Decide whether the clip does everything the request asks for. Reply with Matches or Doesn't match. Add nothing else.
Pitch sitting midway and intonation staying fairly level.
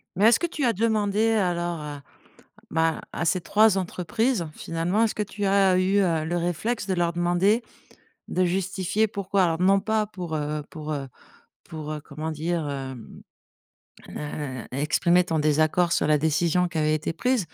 Doesn't match